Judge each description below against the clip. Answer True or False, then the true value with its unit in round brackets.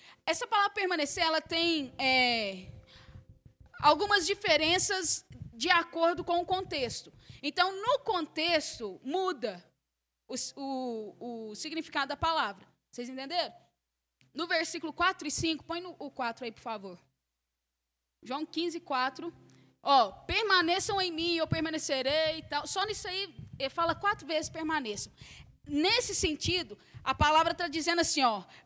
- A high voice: True (320 Hz)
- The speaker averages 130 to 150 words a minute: True (135 wpm)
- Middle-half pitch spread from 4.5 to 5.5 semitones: True (4.8 semitones)